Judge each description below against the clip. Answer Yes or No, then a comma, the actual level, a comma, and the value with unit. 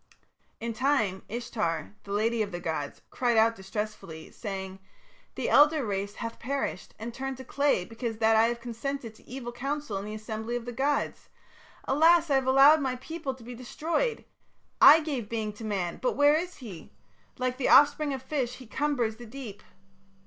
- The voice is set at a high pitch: Yes, high, 240 Hz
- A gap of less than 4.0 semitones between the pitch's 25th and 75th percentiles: No, average, 4.3 semitones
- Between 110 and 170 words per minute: No, average, 185 wpm